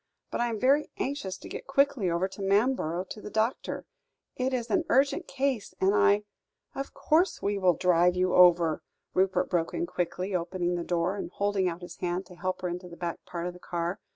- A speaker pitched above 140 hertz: Yes, medium, 185 Hz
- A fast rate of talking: Yes, fast, 215 wpm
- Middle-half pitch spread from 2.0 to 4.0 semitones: No, average, 4.7 semitones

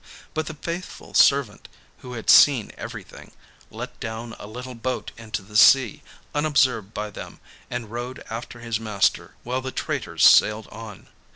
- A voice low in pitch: Yes, low, 115 Hz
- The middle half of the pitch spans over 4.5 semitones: No, average, 3.0 semitones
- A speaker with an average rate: Yes, average, 155 wpm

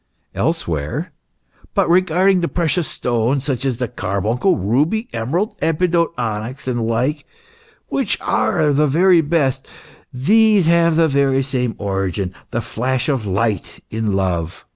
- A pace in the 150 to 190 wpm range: No, average, 140 wpm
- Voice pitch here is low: Yes, low, 130 Hz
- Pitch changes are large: Yes, wide, 7.0 semitones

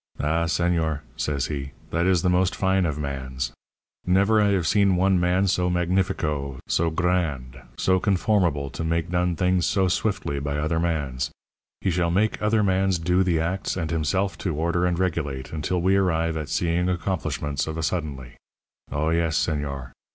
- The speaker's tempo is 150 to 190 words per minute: Yes, average, 180 wpm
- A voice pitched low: Yes, very low, 85 Hz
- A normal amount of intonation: Yes, average, 3.5 semitones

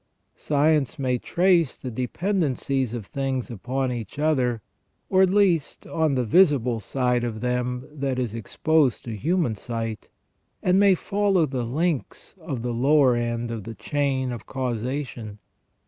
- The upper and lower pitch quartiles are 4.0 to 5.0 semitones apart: Yes, average, 4.5 semitones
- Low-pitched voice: Yes, low, 130 Hz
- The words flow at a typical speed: Yes, average, 145 wpm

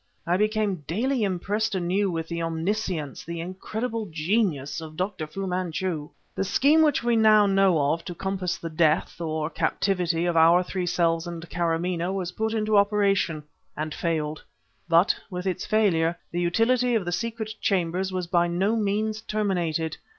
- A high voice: No, medium, 180 Hz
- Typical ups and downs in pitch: Yes, average, 3.9 semitones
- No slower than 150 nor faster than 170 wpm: Yes, average, 160 wpm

